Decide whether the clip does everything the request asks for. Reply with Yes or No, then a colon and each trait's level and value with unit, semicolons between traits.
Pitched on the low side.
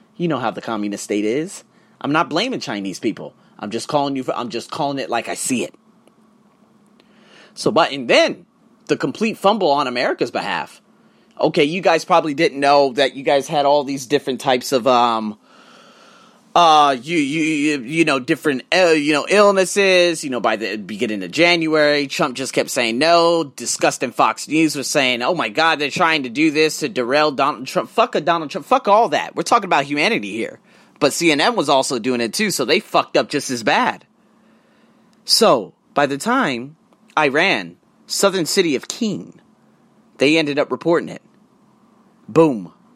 No: medium, 155 Hz